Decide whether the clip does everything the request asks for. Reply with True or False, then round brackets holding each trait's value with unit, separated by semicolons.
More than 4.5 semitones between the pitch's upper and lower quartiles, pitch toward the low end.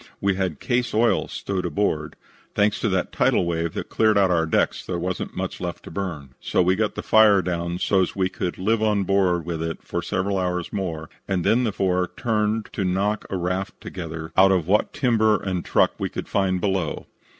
False (2.8 semitones; 95 Hz)